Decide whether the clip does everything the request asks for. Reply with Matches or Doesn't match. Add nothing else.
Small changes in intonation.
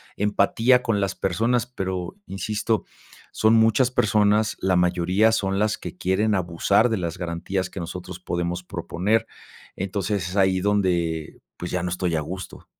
Doesn't match